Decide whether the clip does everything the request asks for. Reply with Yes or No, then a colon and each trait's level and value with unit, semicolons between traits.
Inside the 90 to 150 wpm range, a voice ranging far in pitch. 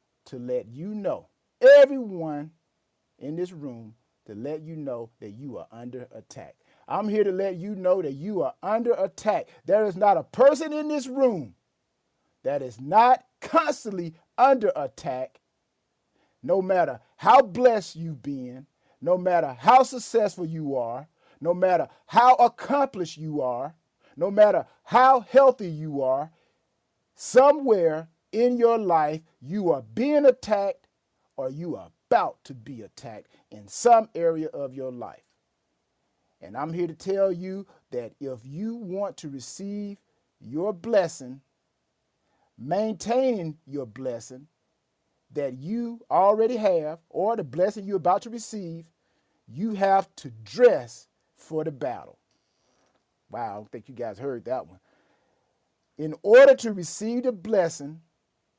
Yes: average, 140 wpm; wide, 6.9 semitones